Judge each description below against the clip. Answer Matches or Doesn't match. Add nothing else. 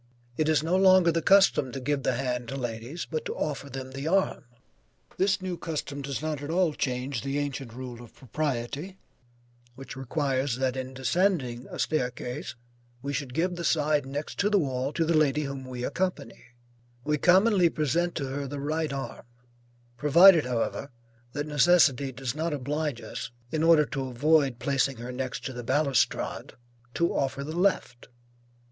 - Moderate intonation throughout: Matches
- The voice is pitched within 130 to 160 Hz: Matches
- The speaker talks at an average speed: Matches